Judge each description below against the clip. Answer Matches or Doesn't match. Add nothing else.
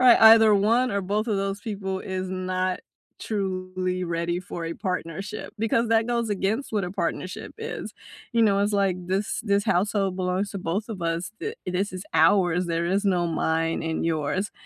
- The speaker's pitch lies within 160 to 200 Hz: Matches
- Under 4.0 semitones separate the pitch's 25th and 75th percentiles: Matches